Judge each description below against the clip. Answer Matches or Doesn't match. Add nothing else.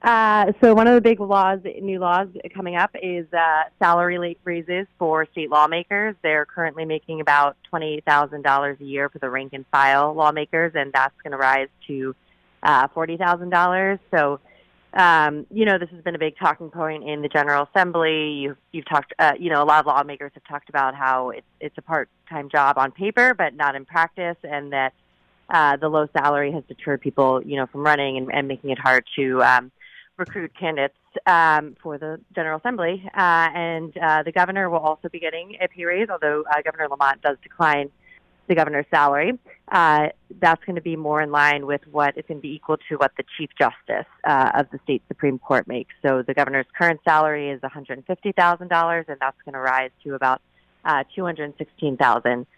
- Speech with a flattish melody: Doesn't match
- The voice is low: Doesn't match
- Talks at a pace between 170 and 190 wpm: Doesn't match